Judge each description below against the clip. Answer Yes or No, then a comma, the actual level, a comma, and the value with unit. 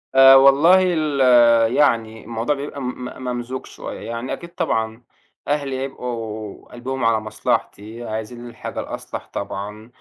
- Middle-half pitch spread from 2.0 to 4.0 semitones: Yes, average, 3.5 semitones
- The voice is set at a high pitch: No, low, 120 Hz